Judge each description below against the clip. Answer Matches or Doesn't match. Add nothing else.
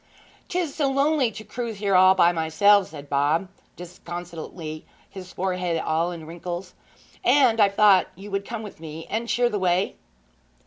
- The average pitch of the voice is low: Doesn't match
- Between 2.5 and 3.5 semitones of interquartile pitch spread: Doesn't match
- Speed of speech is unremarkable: Matches